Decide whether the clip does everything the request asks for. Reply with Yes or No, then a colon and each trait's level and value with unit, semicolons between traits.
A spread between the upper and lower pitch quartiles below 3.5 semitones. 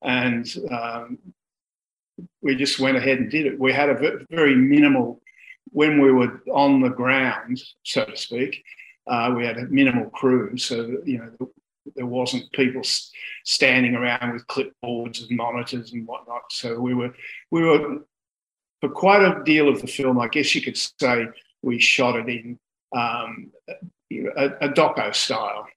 Yes: average, 2.9 semitones